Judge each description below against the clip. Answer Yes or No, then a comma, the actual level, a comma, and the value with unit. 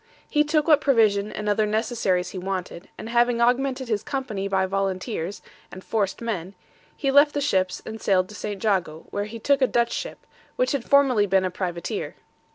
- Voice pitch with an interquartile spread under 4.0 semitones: No, average, 5.2 semitones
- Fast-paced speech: No, average, 190 wpm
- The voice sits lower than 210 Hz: No, high, 215 Hz